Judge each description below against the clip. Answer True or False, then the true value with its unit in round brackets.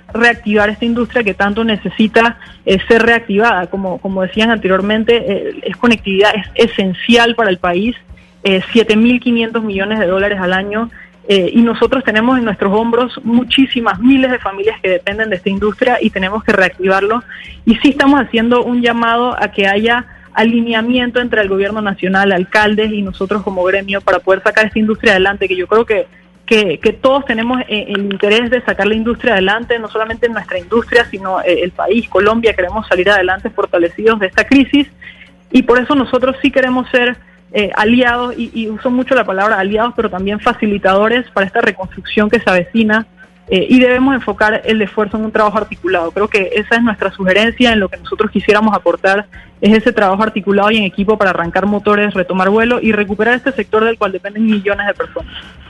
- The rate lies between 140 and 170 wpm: False (185 wpm)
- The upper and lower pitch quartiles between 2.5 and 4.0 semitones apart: True (3.0 semitones)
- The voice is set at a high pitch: True (215 Hz)